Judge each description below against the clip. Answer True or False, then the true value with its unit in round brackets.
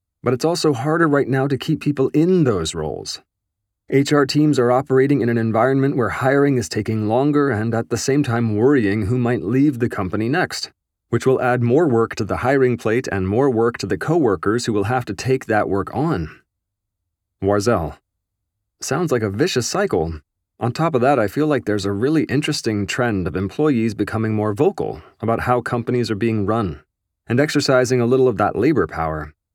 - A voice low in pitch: True (115 Hz)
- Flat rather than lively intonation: False (4.8 semitones)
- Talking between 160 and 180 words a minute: False (195 wpm)